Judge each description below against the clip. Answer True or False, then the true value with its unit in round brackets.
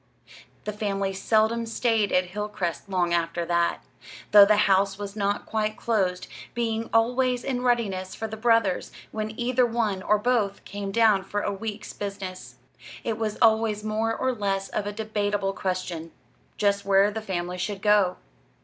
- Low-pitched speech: False (205 Hz)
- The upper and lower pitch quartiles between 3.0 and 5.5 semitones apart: False (2.4 semitones)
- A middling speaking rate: True (160 wpm)